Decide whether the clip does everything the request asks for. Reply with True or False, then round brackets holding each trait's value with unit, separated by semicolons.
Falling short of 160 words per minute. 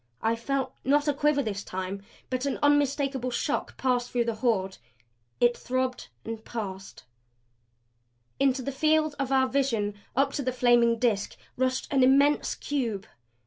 True (150 wpm)